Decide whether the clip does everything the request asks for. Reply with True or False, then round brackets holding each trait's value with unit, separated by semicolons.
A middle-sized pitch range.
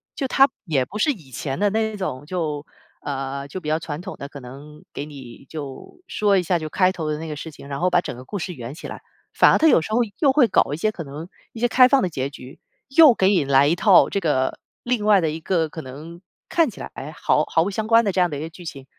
False (6.1 semitones)